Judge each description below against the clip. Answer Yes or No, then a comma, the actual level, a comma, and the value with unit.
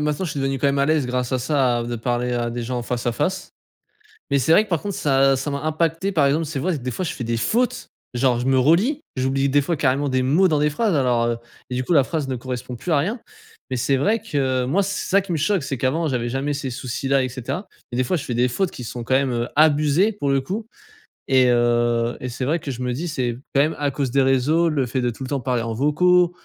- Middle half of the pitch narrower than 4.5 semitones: Yes, average, 4.0 semitones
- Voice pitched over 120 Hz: Yes, low, 135 Hz